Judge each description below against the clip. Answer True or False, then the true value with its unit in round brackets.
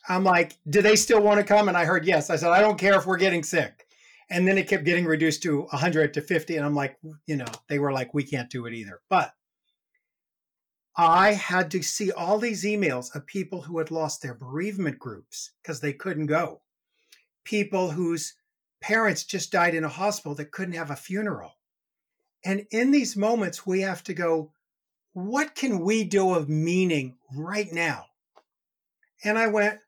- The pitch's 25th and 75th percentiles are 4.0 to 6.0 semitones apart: True (4.8 semitones)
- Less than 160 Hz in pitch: False (180 Hz)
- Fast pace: False (195 wpm)